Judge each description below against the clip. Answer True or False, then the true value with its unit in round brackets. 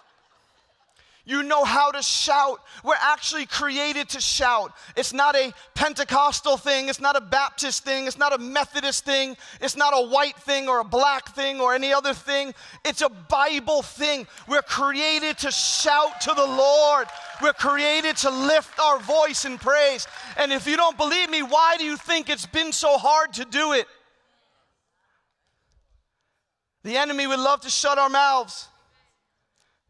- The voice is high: True (285 Hz)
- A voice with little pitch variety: True (1.4 semitones)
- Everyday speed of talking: True (165 wpm)